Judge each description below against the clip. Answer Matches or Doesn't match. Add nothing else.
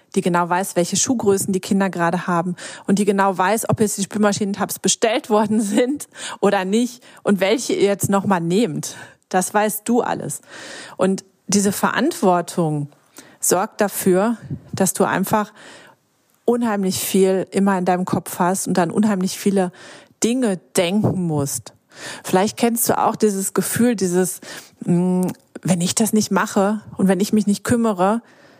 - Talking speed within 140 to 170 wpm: Matches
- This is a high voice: Matches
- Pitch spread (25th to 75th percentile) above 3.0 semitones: Doesn't match